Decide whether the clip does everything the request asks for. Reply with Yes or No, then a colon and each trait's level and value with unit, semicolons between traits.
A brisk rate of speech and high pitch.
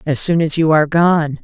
No: fast, 250 wpm; medium, 155 Hz